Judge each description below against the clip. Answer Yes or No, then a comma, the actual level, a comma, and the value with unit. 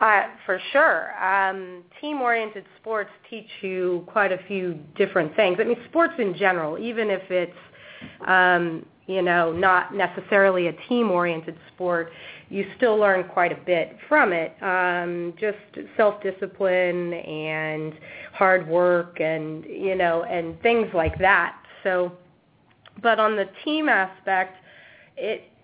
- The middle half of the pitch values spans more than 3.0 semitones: No, average, 2.7 semitones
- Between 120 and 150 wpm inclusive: Yes, average, 140 wpm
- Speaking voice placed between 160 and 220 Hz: Yes, medium, 185 Hz